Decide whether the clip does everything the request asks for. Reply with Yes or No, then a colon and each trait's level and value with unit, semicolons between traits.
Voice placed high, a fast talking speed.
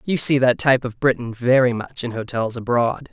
No: low, 125 Hz; fast, 210 wpm